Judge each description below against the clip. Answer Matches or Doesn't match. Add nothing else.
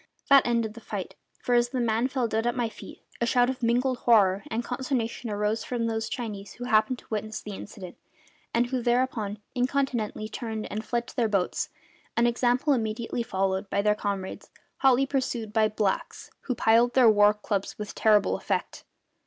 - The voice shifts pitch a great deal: Doesn't match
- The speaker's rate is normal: Matches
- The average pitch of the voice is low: Doesn't match